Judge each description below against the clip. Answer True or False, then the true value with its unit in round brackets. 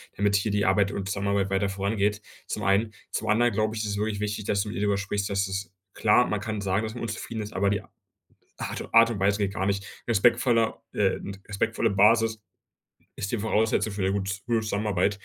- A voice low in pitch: True (105 Hz)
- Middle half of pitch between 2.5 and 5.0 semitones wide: False (1.8 semitones)